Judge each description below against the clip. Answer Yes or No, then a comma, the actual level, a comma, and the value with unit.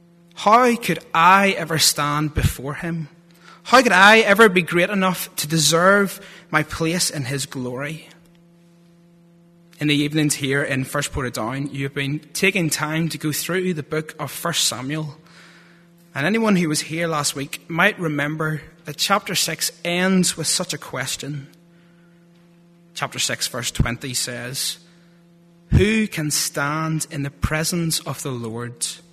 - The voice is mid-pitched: Yes, medium, 165 Hz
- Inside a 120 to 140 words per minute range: No, average, 150 wpm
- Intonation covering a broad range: No, average, 2.9 semitones